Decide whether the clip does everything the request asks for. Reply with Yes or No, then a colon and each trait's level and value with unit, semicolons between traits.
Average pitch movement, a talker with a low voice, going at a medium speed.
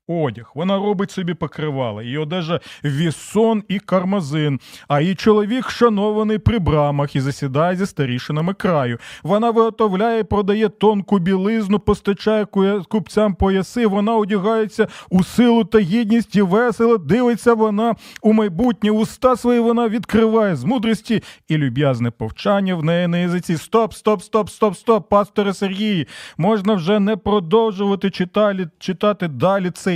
No: average, 3.9 semitones; high, 205 Hz; average, 140 wpm